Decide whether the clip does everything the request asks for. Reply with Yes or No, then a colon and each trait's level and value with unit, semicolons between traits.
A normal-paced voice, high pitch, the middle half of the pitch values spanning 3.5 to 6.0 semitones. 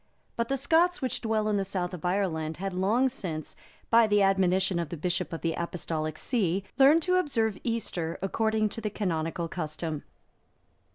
Yes: average, 175 wpm; high, 195 Hz; average, 5.0 semitones